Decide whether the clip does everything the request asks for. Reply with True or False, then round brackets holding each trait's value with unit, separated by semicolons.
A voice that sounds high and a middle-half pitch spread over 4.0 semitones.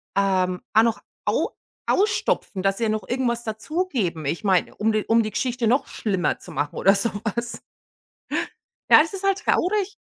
True (220 Hz; 4.6 semitones)